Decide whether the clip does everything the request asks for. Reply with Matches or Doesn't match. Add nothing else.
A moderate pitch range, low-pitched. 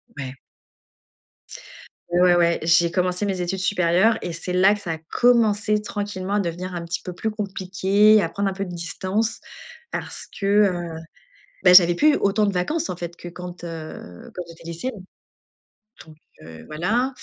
Doesn't match